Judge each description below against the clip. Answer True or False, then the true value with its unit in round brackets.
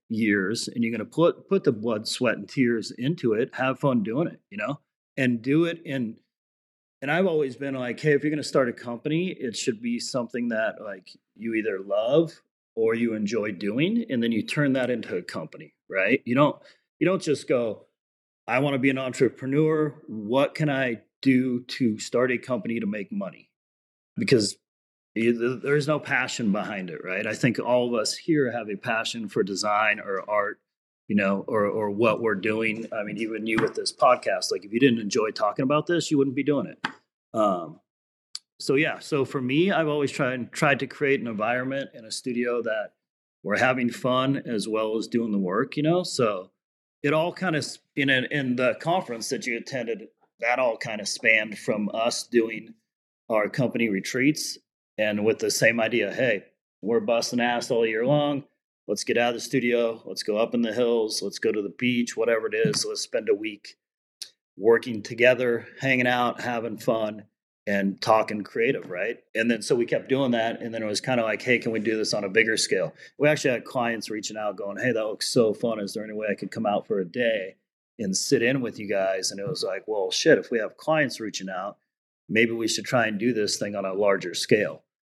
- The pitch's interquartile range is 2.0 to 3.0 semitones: False (4.6 semitones)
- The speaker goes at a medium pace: False (215 wpm)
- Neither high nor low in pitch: False (120 Hz)